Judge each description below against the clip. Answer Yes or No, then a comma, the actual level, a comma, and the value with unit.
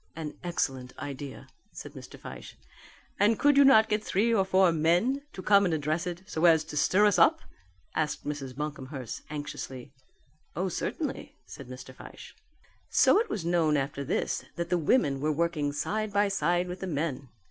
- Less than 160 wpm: No, average, 180 wpm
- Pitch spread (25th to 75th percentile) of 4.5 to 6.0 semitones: Yes, average, 4.8 semitones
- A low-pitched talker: No, medium, 165 Hz